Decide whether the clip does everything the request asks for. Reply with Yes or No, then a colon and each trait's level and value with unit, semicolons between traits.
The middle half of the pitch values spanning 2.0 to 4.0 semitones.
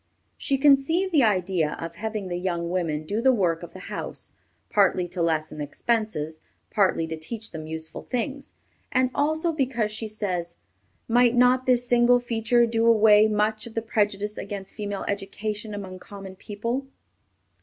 No: average, 4.6 semitones